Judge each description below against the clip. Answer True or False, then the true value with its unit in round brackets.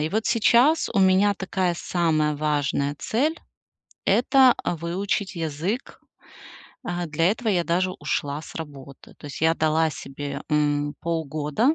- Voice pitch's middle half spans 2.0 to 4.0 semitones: False (4.9 semitones)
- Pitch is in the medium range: True (165 Hz)